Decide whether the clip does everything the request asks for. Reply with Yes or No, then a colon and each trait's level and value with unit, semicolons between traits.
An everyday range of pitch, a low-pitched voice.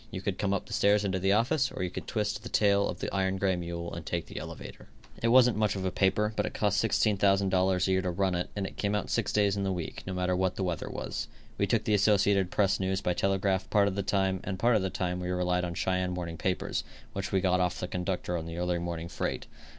No: narrow, 1.9 semitones; very low, 95 Hz